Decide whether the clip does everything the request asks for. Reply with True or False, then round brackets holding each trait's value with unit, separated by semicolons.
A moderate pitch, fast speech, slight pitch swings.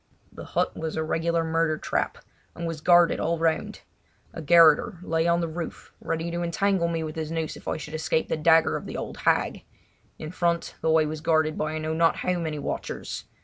True (165 Hz; 215 wpm; 1.2 semitones)